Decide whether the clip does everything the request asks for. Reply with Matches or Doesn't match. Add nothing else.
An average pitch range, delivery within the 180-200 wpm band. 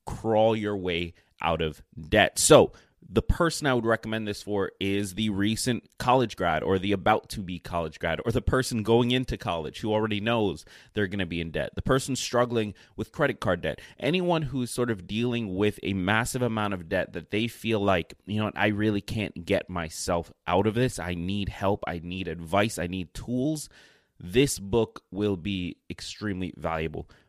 Matches